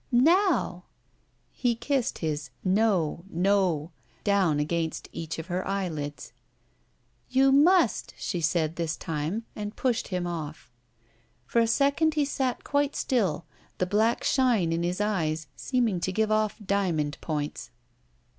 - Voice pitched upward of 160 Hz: Yes, high, 190 Hz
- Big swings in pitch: Yes, wide, 6.5 semitones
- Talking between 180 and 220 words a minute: No, slow, 135 wpm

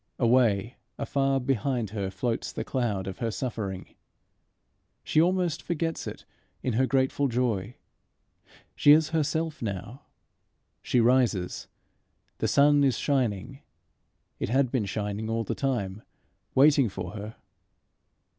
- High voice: No, low, 125 Hz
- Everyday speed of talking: No, slow, 125 wpm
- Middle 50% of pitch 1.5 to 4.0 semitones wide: No, average, 4.8 semitones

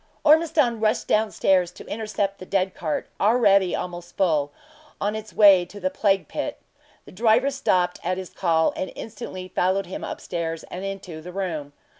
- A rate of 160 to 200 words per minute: Yes, average, 175 wpm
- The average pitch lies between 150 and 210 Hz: Yes, high, 190 Hz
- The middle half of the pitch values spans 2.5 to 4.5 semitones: Yes, average, 3.3 semitones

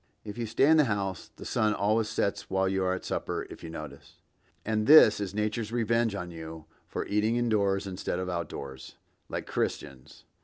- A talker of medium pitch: No, low, 100 Hz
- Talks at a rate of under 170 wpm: No, average, 200 wpm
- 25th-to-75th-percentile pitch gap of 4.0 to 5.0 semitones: No, average, 3.1 semitones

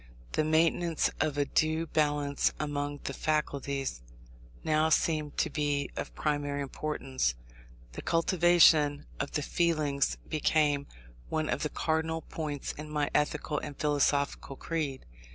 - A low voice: No, medium, 150 Hz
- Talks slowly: Yes, slow, 130 wpm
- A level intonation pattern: Yes, narrow, 1.7 semitones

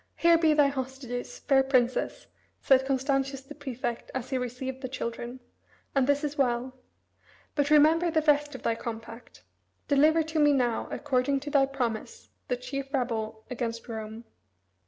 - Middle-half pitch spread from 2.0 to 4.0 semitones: Yes, average, 2.9 semitones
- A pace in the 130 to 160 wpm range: Yes, average, 155 wpm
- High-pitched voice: Yes, very high, 265 Hz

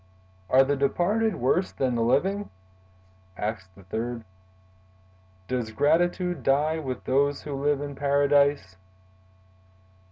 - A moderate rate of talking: No, slow, 115 wpm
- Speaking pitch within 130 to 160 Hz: Yes, medium, 140 Hz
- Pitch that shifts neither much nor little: Yes, average, 3.8 semitones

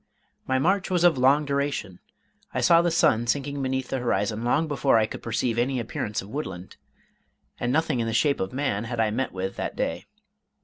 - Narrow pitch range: No, average, 4.4 semitones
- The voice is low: Yes, low, 130 Hz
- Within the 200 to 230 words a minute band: Yes, fast, 205 wpm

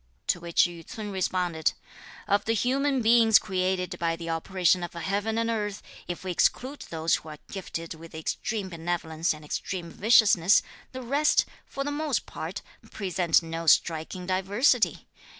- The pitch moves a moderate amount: Yes, average, 4.9 semitones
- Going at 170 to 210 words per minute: No, average, 155 wpm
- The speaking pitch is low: No, medium, 185 Hz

